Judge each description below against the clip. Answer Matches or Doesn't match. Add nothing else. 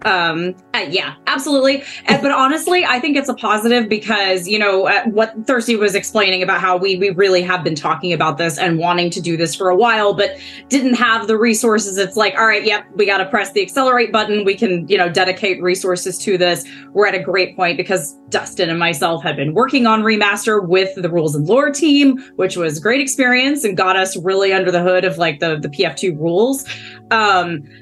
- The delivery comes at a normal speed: Doesn't match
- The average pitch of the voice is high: Matches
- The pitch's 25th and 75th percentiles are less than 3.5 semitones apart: Doesn't match